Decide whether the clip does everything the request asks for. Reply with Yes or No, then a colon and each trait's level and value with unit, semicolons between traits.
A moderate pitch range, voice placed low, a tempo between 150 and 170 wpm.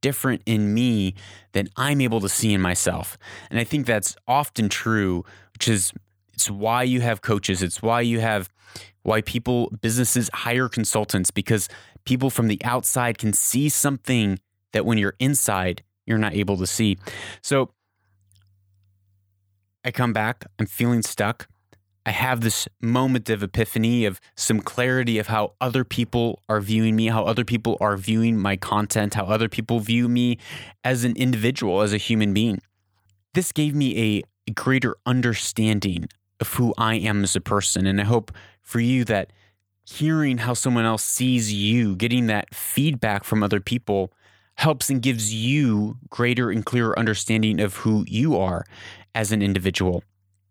Yes: average, 3.4 semitones; low, 110 Hz; average, 165 wpm